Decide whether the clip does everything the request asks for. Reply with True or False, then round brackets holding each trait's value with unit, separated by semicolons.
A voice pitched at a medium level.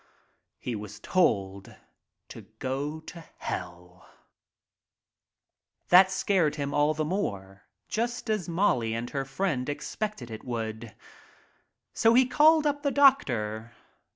True (145 Hz)